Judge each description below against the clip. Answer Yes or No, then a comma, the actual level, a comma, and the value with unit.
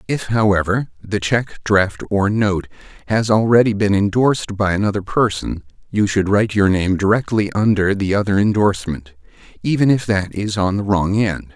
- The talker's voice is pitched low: Yes, low, 100 Hz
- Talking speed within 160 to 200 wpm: Yes, average, 165 wpm